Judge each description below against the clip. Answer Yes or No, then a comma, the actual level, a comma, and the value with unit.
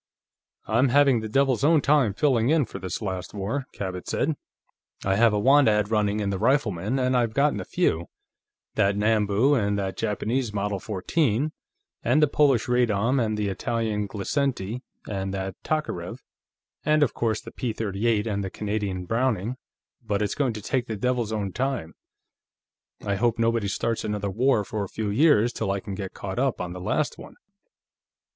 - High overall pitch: No, low, 110 Hz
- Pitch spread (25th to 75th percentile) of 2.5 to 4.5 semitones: Yes, average, 4.1 semitones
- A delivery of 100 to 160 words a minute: No, average, 180 wpm